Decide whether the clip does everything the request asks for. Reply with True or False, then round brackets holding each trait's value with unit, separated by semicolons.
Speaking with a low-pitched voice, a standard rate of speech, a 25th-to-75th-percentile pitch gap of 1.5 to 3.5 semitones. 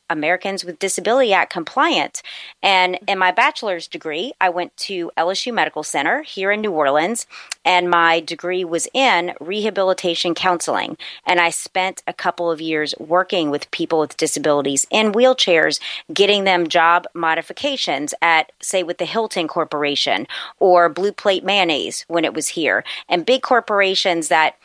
False (180 Hz; 155 wpm; 2.8 semitones)